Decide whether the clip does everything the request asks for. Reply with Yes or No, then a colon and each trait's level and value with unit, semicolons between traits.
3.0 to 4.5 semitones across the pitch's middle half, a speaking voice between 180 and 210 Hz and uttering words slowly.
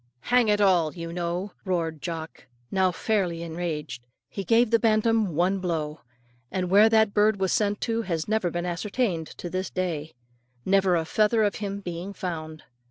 No: average, 3.8 semitones; medium, 185 Hz; average, 170 wpm